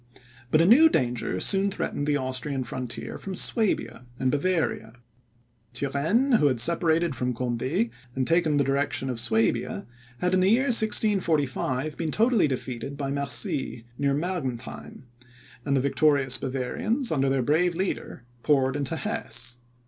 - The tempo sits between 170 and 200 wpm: No, average, 145 wpm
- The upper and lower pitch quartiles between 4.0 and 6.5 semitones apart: Yes, wide, 5.5 semitones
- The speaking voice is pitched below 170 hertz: Yes, medium, 140 Hz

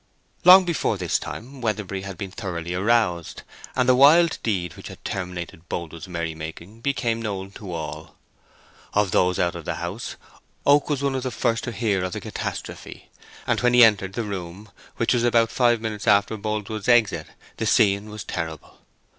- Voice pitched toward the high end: No, low, 105 Hz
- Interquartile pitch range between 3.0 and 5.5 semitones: Yes, average, 4.7 semitones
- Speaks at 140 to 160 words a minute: No, average, 180 wpm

